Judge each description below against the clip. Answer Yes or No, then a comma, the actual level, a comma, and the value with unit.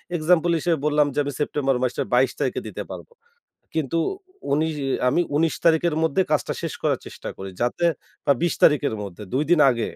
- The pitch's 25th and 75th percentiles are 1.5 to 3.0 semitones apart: No, average, 3.7 semitones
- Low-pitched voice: No, medium, 150 Hz